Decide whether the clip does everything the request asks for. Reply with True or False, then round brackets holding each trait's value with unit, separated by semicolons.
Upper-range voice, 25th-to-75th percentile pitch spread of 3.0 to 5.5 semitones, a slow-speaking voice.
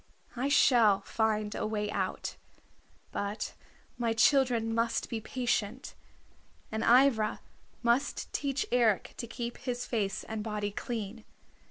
False (230 Hz; 2.5 semitones; 125 wpm)